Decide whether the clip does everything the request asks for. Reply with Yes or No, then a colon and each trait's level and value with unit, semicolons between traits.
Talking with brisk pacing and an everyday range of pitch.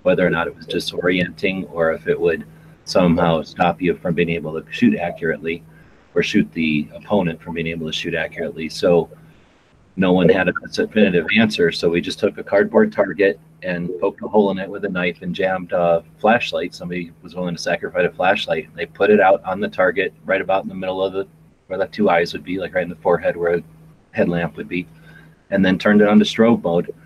Yes: fast, 225 wpm; average, 3.1 semitones